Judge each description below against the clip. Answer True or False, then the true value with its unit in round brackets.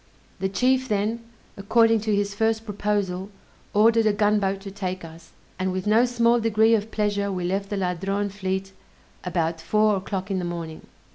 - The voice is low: False (200 Hz)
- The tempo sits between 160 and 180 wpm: True (170 wpm)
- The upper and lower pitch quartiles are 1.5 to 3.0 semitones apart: True (2.5 semitones)